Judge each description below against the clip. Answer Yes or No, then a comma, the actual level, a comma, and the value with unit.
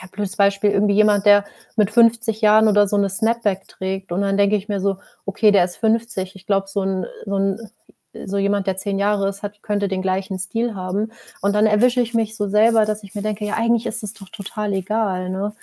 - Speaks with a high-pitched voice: Yes, high, 205 Hz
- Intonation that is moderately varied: No, narrow, 1.7 semitones